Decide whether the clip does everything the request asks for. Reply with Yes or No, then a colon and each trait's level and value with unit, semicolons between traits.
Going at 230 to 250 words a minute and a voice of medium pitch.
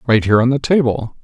No: fast, 245 wpm; low, 125 Hz